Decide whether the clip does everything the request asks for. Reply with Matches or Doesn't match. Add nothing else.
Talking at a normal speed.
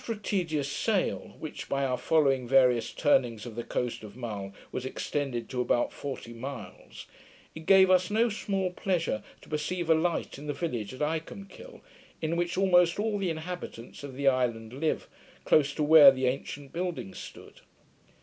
Matches